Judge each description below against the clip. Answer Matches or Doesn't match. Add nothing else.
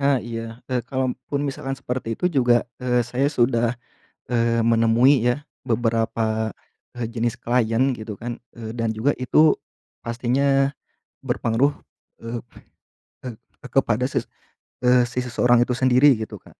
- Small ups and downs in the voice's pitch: Matches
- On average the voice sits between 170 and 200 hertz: Doesn't match